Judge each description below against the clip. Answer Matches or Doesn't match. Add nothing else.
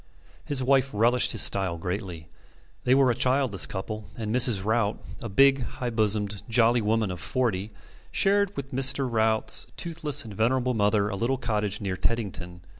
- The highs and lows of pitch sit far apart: Doesn't match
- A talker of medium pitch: Doesn't match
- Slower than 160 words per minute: Doesn't match